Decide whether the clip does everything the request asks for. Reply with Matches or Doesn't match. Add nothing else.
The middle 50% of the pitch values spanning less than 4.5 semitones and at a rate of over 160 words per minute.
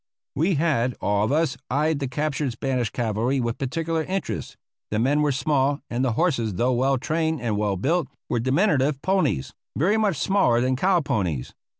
Doesn't match